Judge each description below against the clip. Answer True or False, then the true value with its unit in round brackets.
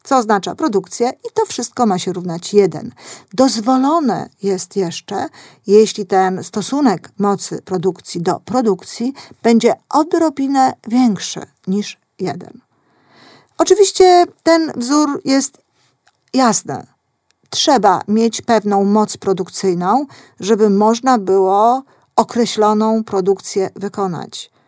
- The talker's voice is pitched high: True (220 Hz)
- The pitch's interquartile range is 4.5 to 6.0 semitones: True (5.2 semitones)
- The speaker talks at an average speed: False (100 wpm)